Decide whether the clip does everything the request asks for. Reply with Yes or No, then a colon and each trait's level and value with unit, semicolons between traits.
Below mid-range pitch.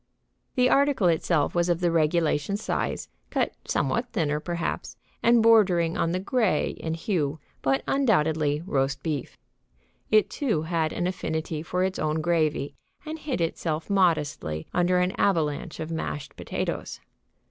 No: medium, 170 Hz